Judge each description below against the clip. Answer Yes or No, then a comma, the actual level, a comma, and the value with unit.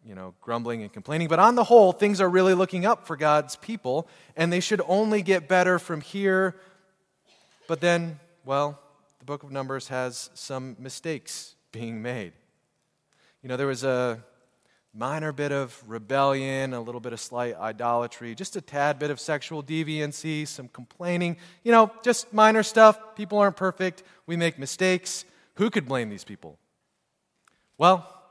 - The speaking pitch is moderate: Yes, medium, 155 Hz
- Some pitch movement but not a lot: No, wide, 6.4 semitones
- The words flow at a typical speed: Yes, average, 165 wpm